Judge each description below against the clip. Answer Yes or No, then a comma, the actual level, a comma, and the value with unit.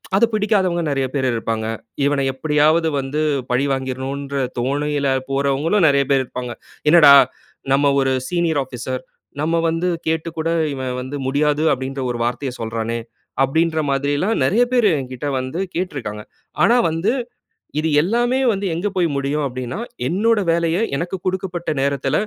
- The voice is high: No, medium, 145 Hz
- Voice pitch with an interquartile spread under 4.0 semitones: No, average, 4.3 semitones